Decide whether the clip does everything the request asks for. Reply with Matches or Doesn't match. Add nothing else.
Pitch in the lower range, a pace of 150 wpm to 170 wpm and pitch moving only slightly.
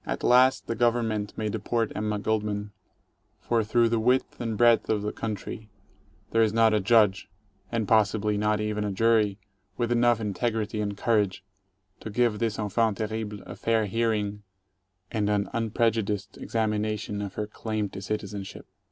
Matches